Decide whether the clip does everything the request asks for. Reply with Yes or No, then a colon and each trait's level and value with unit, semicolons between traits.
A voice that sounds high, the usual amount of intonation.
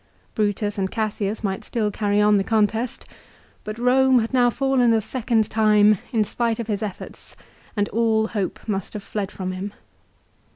No: high, 215 Hz; narrow, 2.0 semitones